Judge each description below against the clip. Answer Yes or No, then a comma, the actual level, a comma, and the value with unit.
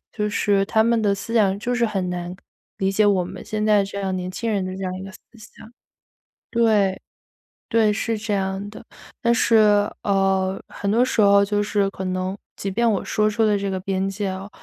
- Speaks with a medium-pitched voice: No, high, 200 Hz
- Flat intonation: Yes, narrow, 2.0 semitones